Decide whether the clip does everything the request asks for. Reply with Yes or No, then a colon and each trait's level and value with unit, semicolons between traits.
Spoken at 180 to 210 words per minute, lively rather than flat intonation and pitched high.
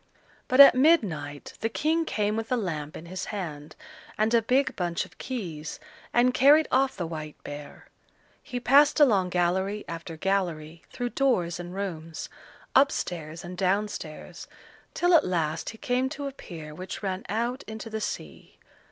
No: average, 170 wpm; wide, 7.0 semitones; high, 195 Hz